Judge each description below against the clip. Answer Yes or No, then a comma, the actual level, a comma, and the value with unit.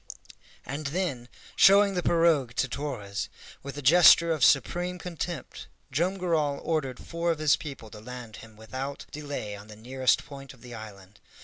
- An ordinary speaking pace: Yes, average, 170 wpm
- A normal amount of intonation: No, wide, 5.9 semitones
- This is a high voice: No, medium, 140 Hz